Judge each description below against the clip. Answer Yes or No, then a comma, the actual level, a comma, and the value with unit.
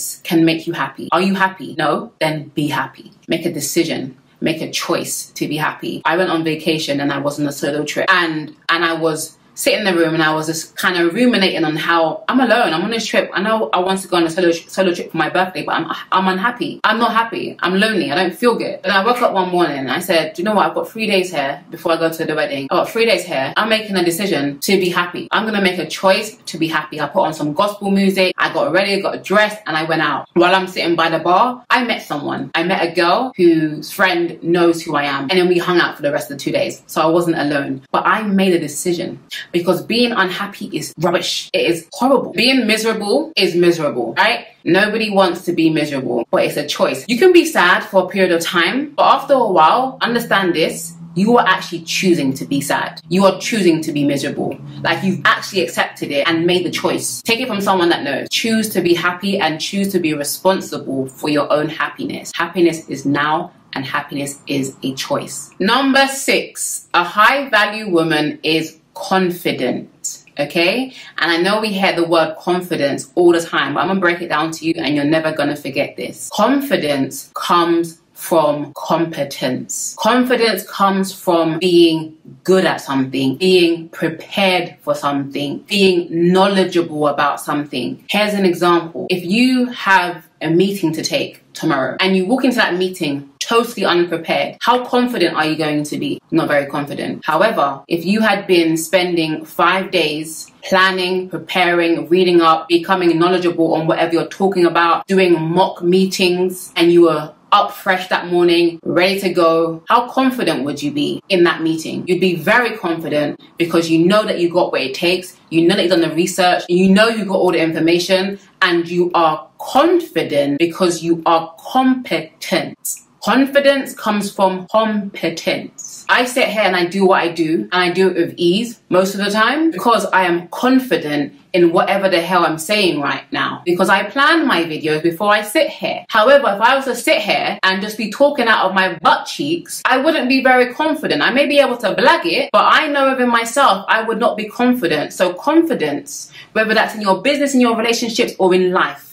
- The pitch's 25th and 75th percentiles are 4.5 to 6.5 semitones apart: No, average, 3.9 semitones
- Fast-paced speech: Yes, fast, 210 wpm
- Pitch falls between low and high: Yes, medium, 180 Hz